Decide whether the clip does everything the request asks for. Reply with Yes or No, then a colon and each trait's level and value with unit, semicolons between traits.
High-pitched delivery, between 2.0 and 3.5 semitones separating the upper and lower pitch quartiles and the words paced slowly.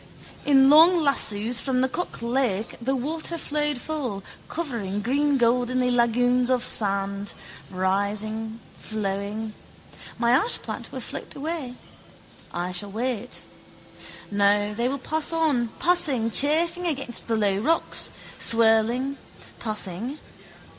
No: high, 245 Hz; average, 4.9 semitones; slow, 115 wpm